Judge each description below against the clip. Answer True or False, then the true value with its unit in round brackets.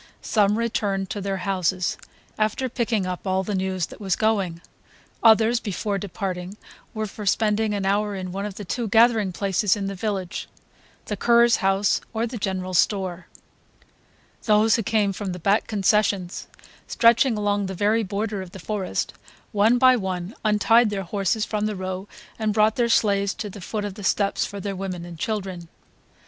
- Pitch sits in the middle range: False (205 Hz)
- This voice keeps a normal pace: True (180 wpm)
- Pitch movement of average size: False (2.3 semitones)